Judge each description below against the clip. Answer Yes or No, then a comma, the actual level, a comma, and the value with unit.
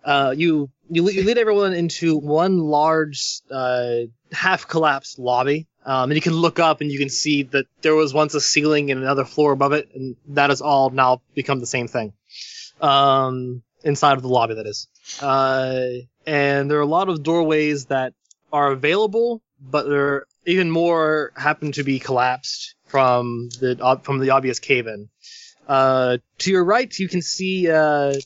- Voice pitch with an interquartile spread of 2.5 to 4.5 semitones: Yes, average, 3.2 semitones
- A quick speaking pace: No, average, 180 wpm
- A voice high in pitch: No, medium, 140 Hz